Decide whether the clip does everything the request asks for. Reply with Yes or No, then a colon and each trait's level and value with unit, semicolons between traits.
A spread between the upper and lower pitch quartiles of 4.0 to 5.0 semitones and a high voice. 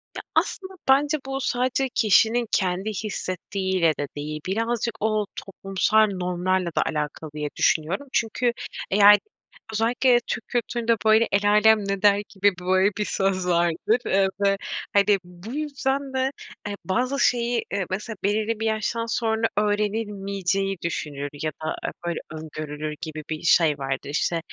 Yes: average, 4.3 semitones; high, 200 Hz